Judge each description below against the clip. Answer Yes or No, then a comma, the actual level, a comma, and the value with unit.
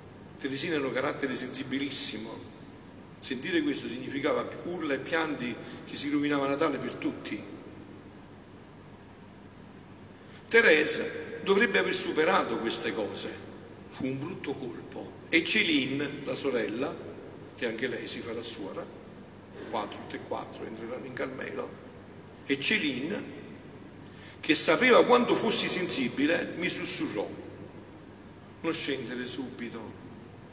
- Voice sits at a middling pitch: No, low, 125 Hz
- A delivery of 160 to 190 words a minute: No, slow, 115 wpm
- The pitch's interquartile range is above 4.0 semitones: Yes, wide, 5.5 semitones